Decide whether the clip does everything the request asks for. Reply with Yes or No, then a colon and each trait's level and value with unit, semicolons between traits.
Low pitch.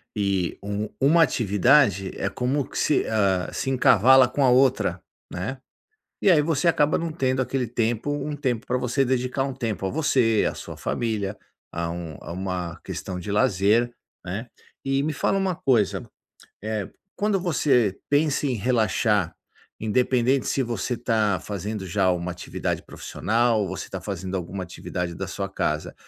Yes: low, 115 Hz